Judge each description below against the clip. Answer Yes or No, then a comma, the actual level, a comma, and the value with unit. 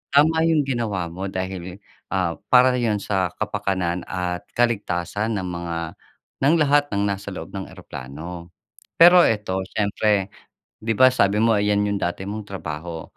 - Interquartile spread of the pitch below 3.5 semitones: No, average, 4.3 semitones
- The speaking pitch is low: Yes, low, 100 Hz